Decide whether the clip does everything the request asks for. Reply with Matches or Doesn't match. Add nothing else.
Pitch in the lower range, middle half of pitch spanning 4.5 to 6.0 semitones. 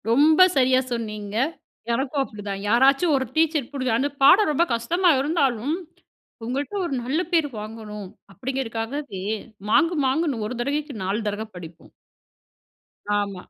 Doesn't match